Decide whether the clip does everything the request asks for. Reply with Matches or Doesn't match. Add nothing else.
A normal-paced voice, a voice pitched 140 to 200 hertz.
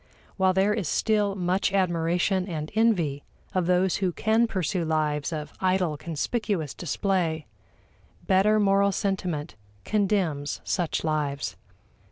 Doesn't match